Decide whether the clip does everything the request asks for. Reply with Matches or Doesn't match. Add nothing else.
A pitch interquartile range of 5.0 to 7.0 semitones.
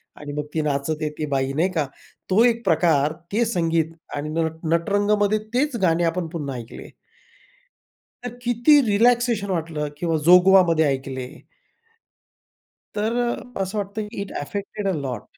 Matches